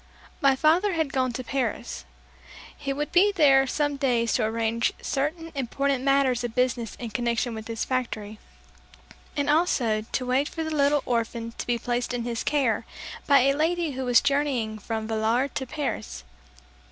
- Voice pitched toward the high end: Yes, very high, 255 Hz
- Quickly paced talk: No, average, 170 wpm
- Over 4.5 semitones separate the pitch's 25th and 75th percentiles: No, average, 3.6 semitones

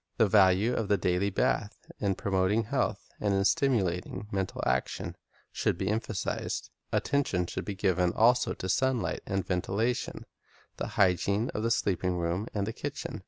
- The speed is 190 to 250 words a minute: No, average, 165 wpm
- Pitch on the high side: No, low, 100 Hz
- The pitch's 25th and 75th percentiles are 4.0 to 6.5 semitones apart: No, average, 3.2 semitones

